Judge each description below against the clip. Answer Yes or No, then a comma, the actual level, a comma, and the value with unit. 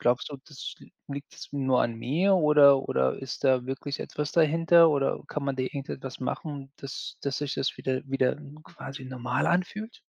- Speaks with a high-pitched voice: No, medium, 140 Hz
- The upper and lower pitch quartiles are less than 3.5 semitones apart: Yes, narrow, 2.4 semitones